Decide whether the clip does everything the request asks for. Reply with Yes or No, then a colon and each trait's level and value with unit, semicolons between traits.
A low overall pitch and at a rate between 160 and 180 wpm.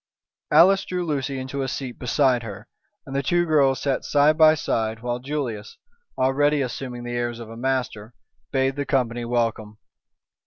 Yes: low, 130 Hz; average, 165 wpm